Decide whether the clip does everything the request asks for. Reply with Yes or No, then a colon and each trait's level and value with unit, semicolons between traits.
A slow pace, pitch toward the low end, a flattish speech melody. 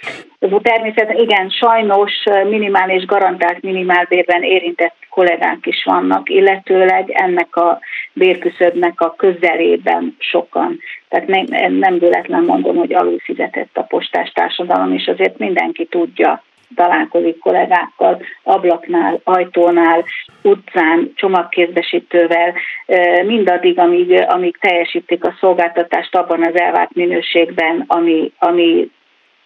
No: slow, 100 wpm; medium, 175 Hz; narrow, 2.2 semitones